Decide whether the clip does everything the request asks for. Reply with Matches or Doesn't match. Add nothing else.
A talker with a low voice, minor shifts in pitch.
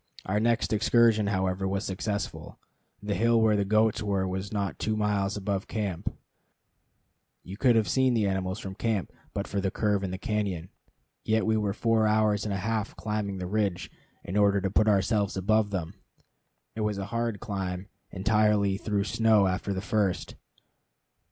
Matches